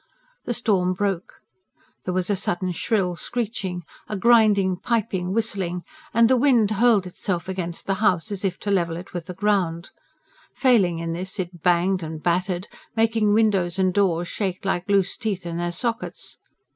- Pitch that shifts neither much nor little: Yes, average, 3.1 semitones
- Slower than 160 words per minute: No, average, 170 wpm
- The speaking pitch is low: No, high, 190 Hz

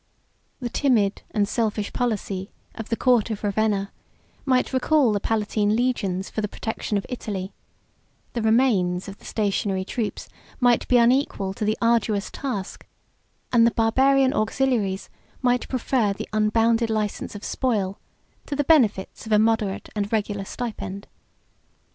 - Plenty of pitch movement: No, average, 3.3 semitones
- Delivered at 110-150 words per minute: Yes, average, 145 wpm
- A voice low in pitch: No, high, 220 Hz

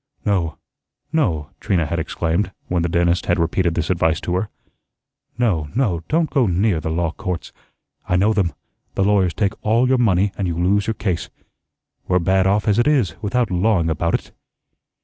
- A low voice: Yes, very low, 90 Hz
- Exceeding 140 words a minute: Yes, average, 185 wpm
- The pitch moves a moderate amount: Yes, average, 3.8 semitones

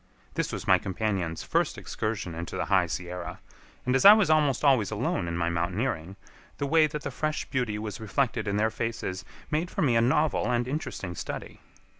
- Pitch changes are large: Yes, wide, 7.0 semitones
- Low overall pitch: Yes, low, 110 Hz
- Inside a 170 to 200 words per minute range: Yes, average, 195 wpm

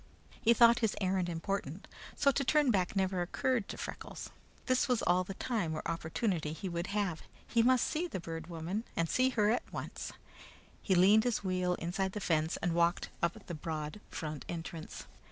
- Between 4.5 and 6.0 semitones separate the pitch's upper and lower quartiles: Yes, average, 4.9 semitones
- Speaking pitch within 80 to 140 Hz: No, medium, 185 Hz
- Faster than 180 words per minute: Yes, average, 190 wpm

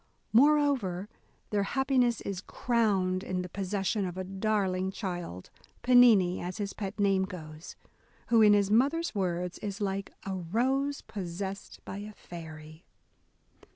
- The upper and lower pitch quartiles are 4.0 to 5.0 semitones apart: No, average, 3.3 semitones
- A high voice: Yes, high, 195 Hz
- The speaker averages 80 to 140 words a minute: Yes, slow, 135 wpm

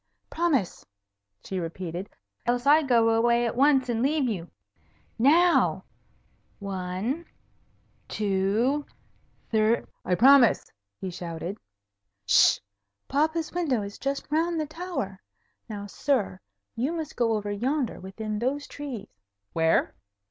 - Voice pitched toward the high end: Yes, high, 235 Hz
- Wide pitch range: Yes, wide, 6.3 semitones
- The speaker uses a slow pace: Yes, slow, 120 wpm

